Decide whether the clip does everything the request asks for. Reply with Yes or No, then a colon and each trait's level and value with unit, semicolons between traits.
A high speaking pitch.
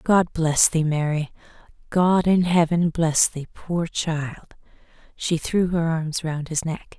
No: medium, 165 Hz